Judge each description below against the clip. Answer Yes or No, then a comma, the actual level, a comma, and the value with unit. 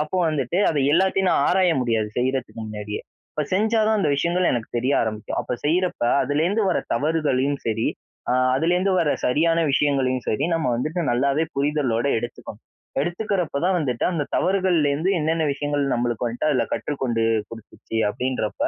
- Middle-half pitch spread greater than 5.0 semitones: Yes, wide, 5.6 semitones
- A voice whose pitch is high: No, medium, 145 Hz